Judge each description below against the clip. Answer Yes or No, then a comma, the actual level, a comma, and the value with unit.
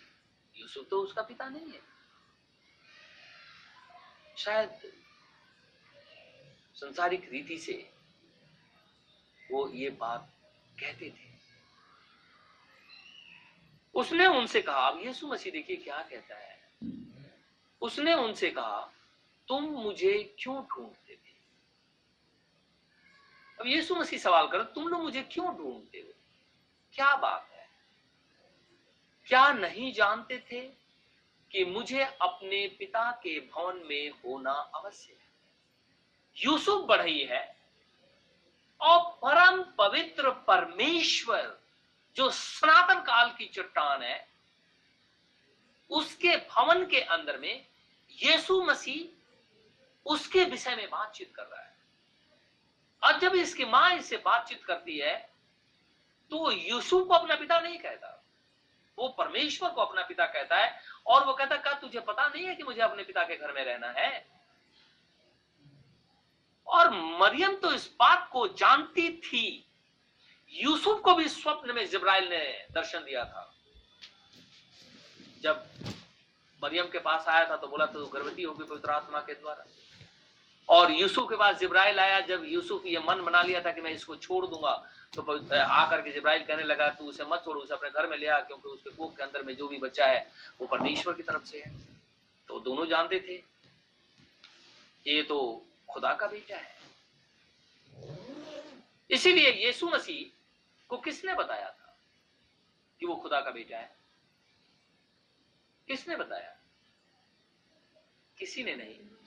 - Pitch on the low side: No, very high, 270 Hz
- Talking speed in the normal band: Yes, average, 130 wpm